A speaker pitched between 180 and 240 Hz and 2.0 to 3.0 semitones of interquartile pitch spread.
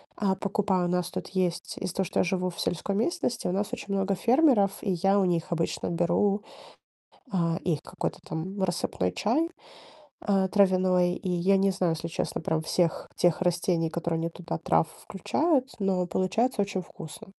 Yes: medium, 185 Hz; narrow, 2.5 semitones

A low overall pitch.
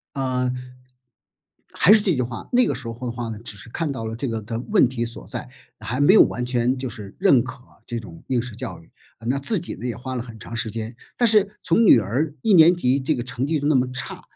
Yes: low, 125 Hz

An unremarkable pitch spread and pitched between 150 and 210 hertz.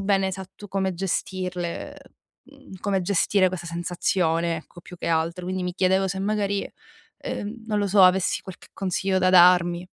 No: narrow, 1.8 semitones; medium, 185 Hz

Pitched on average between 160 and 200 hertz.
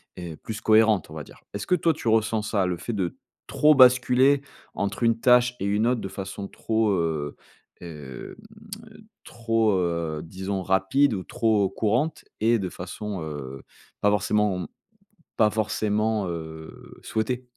No: low, 105 Hz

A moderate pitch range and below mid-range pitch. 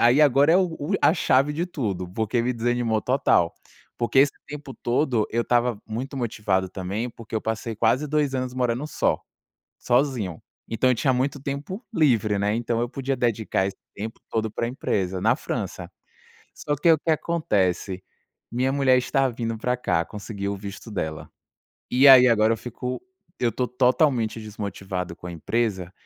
Yes: average, 4.0 semitones; low, 120 Hz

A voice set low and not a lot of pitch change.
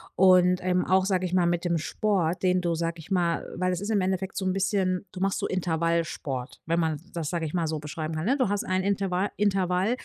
No: medium, 180 Hz; narrow, 2.2 semitones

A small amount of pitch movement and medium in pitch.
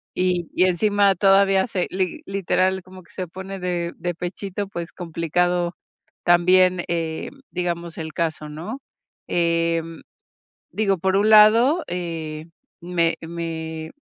Yes: narrow, 2.3 semitones; medium, 180 Hz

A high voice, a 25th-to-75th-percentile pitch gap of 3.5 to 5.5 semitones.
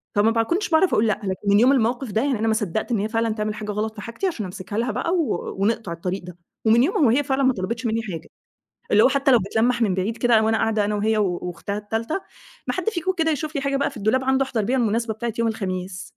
Yes: high, 225 Hz; average, 3.9 semitones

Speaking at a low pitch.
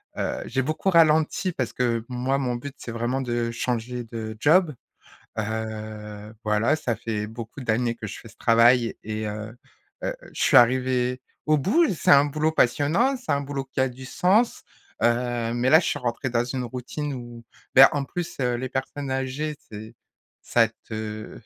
Yes: low, 125 Hz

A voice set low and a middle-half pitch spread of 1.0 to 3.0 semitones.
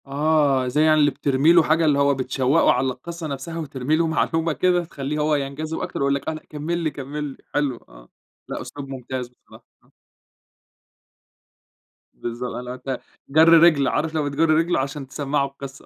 No: medium, 145 Hz; average, 2.7 semitones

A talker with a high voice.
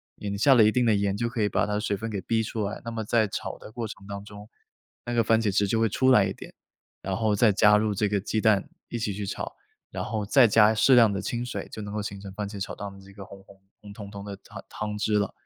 No: low, 105 Hz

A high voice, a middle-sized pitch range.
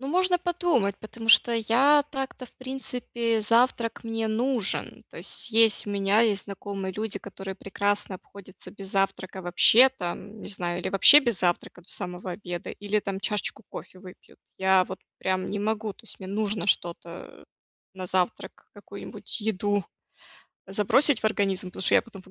Yes: high, 205 Hz; average, 3.2 semitones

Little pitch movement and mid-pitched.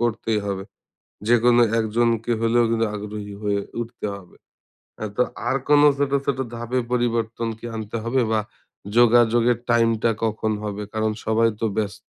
No: narrow, 1.7 semitones; low, 115 Hz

